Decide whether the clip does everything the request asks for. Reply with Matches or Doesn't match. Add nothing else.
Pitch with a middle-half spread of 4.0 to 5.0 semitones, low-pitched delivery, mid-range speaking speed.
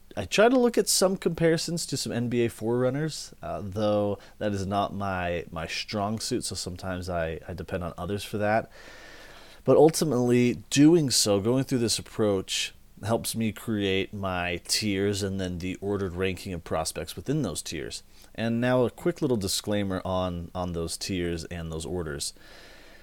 Matches